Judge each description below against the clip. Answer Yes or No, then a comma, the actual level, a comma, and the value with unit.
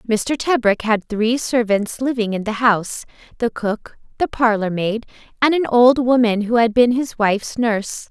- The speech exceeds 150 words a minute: Yes, average, 180 wpm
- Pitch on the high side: Yes, high, 230 Hz